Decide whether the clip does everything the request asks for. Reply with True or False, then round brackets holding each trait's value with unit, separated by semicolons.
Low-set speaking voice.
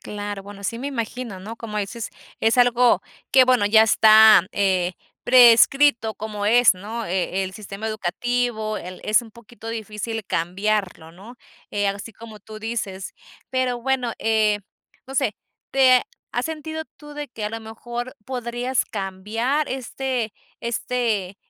False (225 Hz)